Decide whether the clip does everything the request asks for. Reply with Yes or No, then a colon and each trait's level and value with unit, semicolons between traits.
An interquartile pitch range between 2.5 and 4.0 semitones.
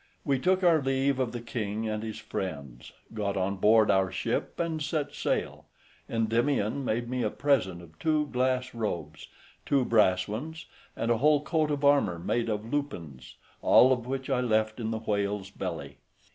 No: average, 5.1 semitones